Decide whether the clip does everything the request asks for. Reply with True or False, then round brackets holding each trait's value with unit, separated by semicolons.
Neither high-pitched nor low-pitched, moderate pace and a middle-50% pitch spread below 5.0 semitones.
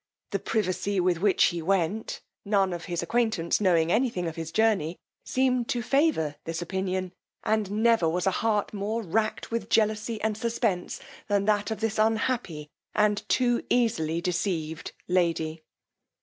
False (200 Hz; 155 wpm; 4.3 semitones)